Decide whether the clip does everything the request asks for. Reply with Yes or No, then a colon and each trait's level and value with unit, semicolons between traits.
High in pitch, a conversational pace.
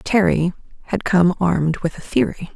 No: medium, 180 Hz; average, 165 wpm